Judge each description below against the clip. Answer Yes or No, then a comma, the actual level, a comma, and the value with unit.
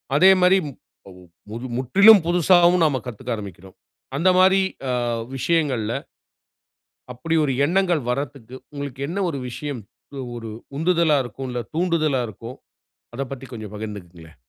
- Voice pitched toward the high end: No, low, 135 Hz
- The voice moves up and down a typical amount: No, wide, 6.3 semitones